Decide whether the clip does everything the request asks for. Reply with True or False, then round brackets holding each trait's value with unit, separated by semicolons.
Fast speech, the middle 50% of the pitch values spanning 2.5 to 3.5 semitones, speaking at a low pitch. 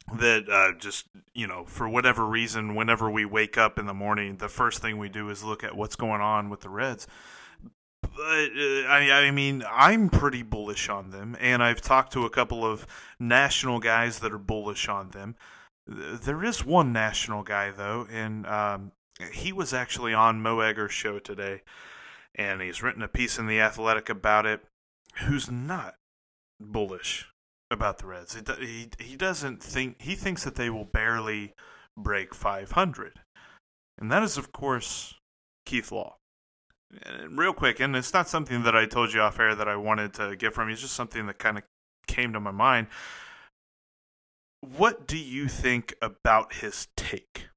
False (175 wpm; 3.2 semitones; 115 Hz)